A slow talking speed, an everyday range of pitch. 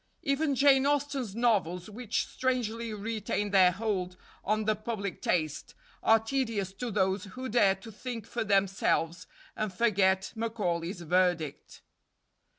Yes: slow, 130 wpm; average, 3.8 semitones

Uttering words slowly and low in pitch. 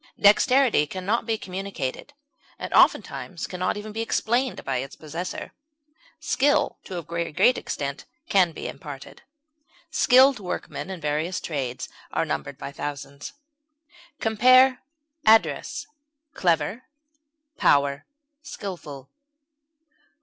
No: slow, 115 wpm; medium, 185 Hz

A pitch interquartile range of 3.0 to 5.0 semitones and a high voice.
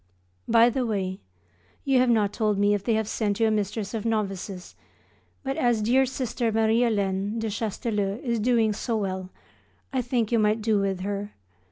No: narrow, 2.5 semitones; high, 220 Hz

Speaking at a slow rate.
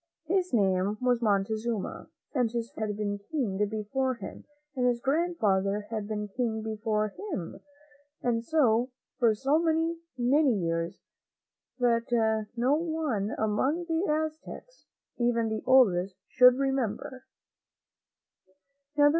Yes: slow, 120 wpm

